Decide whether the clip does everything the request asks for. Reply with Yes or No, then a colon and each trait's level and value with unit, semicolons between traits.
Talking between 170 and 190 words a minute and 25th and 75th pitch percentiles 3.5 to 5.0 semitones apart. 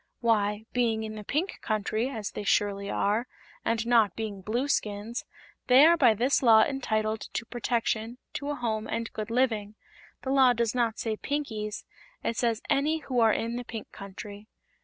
No: average, 175 wpm; narrow, 2.5 semitones